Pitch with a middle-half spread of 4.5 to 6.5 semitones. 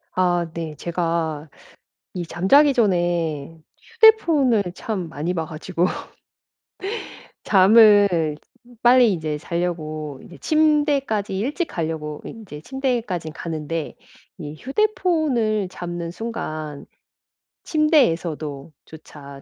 No: wide, 6.9 semitones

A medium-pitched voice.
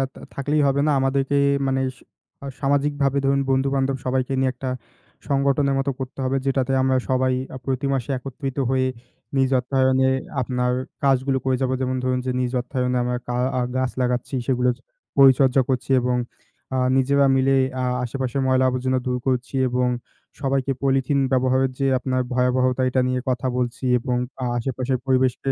No: low, 130 Hz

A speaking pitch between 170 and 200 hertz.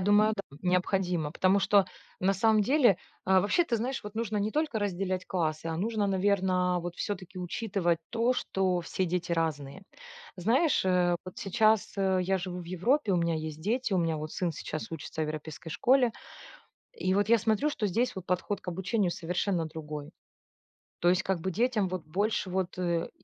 Yes: medium, 185 Hz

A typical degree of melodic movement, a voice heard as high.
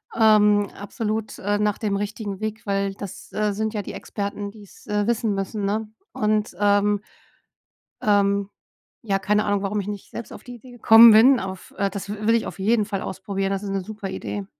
No: narrow, 1.5 semitones; high, 205 Hz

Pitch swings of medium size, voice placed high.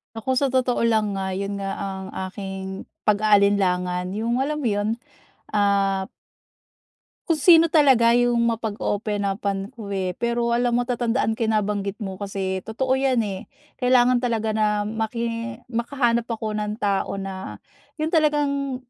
Yes: average, 3.6 semitones; high, 220 Hz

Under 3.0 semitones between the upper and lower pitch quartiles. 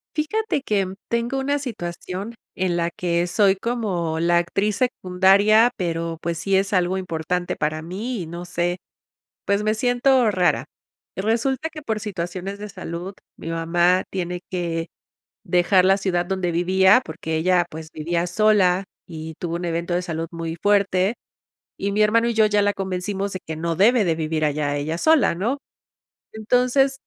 No: average, 3.8 semitones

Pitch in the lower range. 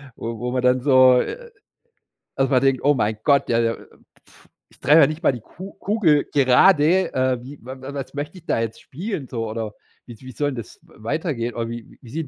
Yes: low, 130 Hz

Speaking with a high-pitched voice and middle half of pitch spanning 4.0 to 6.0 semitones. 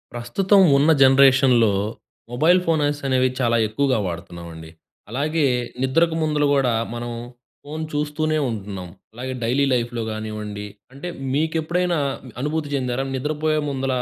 No: low, 135 Hz; average, 4.6 semitones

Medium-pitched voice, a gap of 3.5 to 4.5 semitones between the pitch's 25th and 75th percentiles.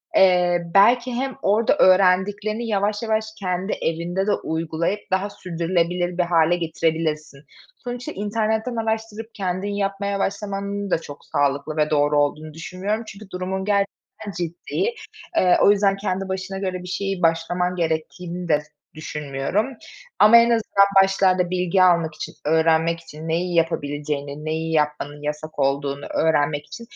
Yes: medium, 180 Hz; average, 3.9 semitones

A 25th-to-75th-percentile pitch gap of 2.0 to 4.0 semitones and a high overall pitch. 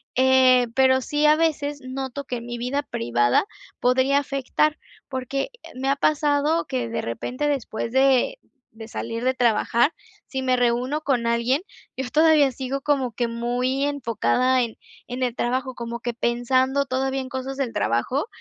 Yes: narrow, 2.6 semitones; very high, 260 Hz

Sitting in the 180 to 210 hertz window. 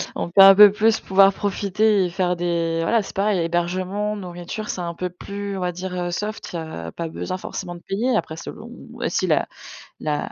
Yes: medium, 185 Hz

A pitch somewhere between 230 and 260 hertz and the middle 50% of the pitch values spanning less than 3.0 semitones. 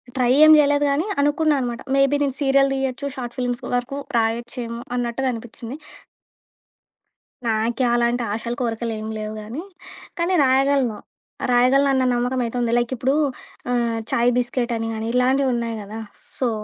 Yes: high, 245 Hz; narrow, 2.5 semitones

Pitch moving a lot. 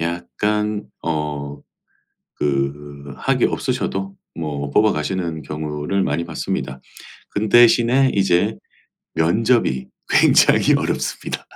Yes: wide, 6.1 semitones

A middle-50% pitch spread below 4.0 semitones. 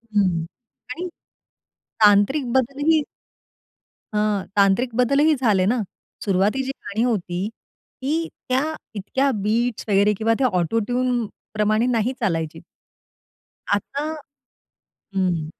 No: average, 4.4 semitones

